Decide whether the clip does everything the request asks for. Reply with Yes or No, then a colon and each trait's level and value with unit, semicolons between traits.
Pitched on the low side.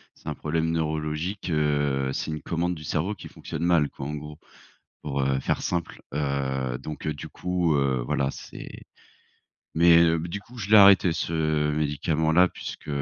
Yes: very low, 80 Hz